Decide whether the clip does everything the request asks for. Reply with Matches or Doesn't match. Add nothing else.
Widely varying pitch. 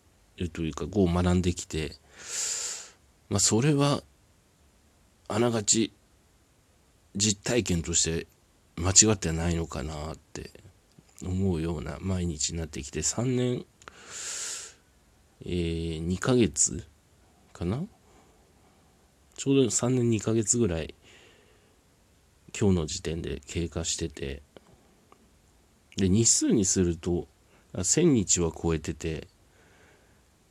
Doesn't match